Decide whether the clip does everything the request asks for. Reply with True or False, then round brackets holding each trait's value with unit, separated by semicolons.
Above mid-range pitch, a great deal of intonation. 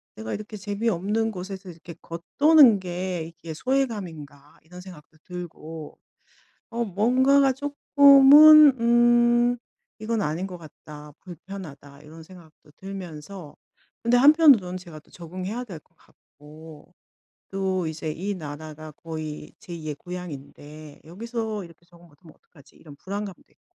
False (180 Hz; 6.2 semitones)